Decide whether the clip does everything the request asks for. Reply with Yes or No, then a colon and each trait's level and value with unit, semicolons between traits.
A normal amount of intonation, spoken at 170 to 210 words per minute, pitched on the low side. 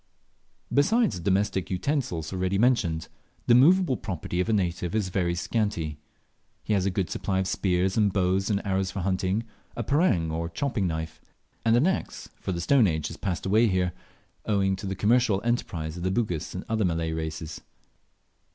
Yes: average, 4.1 semitones; average, 180 wpm; very low, 95 Hz